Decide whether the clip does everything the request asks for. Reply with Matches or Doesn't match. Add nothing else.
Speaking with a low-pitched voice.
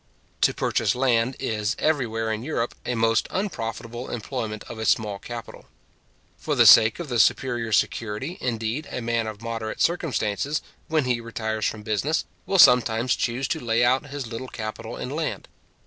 Matches